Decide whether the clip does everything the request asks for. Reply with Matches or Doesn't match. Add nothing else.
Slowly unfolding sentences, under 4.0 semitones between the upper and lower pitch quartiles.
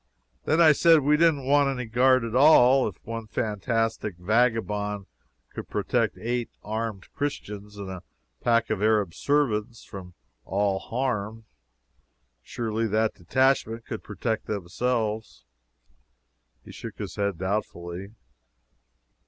Matches